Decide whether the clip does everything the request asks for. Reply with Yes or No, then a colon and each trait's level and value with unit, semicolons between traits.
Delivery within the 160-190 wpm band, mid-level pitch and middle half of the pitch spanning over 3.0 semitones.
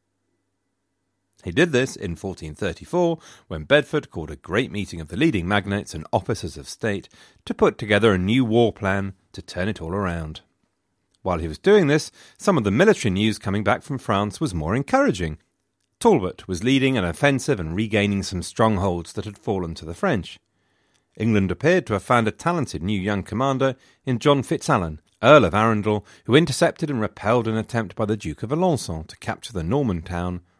No: average, 185 wpm; low, 105 Hz; wide, 5.6 semitones